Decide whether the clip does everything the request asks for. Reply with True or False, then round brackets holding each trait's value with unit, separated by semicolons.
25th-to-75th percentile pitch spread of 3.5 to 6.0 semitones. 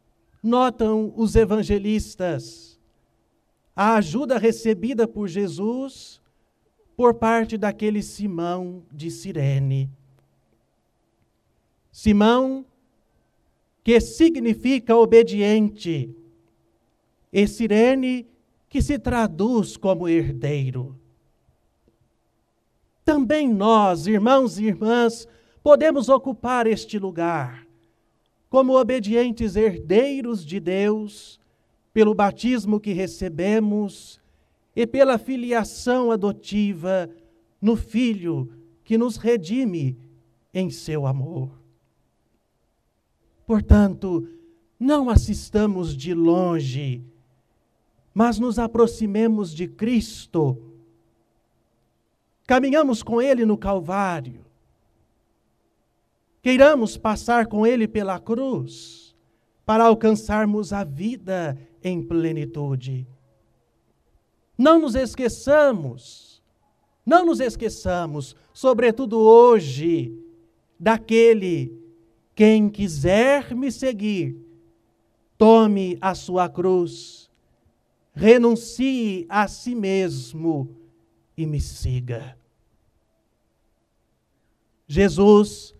False (7.2 semitones)